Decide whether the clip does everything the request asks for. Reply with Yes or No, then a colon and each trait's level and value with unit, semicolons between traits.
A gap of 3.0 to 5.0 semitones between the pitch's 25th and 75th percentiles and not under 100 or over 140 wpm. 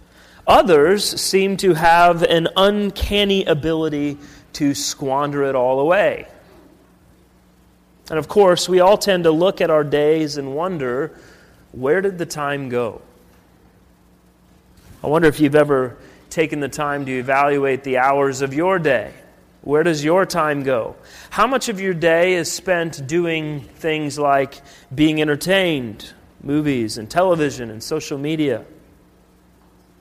Yes: average, 3.7 semitones; slow, 135 wpm